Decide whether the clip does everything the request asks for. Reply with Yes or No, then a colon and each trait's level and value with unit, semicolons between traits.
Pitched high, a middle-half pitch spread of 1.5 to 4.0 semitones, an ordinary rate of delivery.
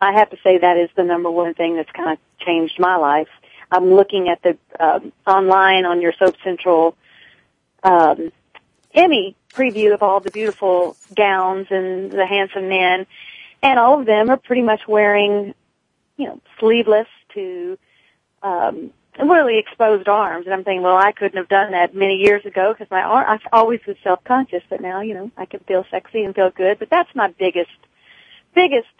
Yes: high, 195 Hz; average, 2.7 semitones; average, 185 wpm